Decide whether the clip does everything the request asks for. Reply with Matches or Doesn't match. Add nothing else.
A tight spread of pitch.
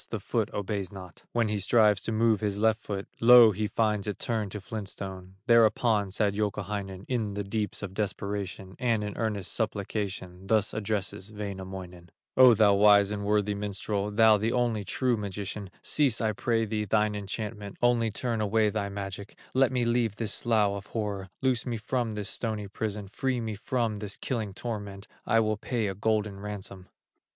Matches